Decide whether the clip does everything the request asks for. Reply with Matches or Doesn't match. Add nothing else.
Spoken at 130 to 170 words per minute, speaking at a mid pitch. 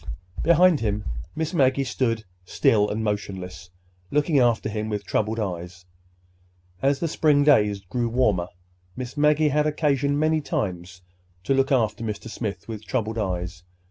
Doesn't match